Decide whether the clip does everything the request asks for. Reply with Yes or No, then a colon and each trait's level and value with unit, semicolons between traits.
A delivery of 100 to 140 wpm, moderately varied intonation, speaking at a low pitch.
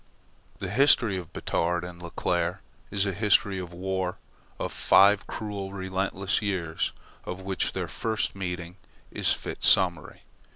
No: slow, 135 wpm; narrow, 2.0 semitones; very low, 95 Hz